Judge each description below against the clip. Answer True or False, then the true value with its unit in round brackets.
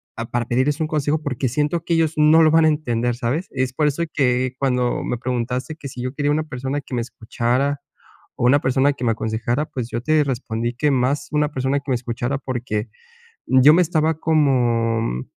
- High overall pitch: False (130 Hz)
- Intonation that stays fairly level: False (3.6 semitones)